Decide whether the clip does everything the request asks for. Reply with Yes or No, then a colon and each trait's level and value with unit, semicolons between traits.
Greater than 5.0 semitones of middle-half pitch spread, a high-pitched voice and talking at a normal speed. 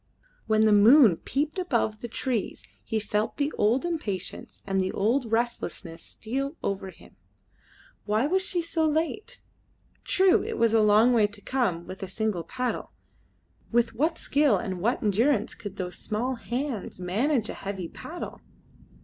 Yes: wide, 5.4 semitones; high, 225 Hz; average, 160 wpm